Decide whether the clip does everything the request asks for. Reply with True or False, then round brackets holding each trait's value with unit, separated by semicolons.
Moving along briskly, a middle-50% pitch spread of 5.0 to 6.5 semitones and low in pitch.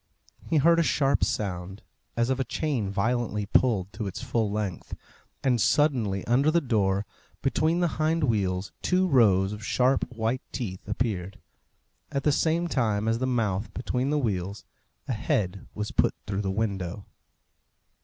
False (160 wpm; 5.3 semitones; 115 Hz)